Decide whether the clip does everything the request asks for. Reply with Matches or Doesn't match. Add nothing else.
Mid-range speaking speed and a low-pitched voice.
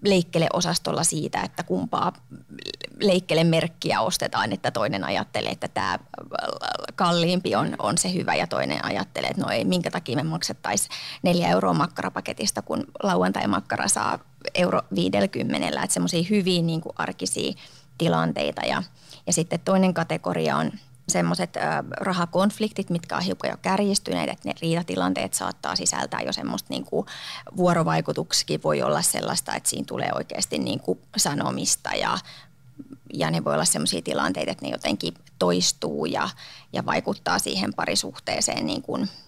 Doesn't match